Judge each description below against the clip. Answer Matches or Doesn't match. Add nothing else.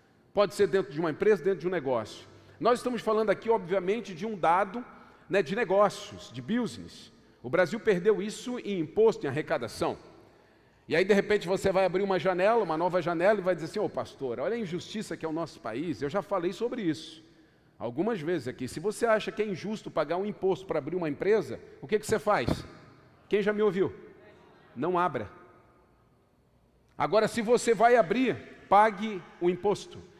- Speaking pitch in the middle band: Doesn't match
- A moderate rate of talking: Doesn't match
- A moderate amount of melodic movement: Matches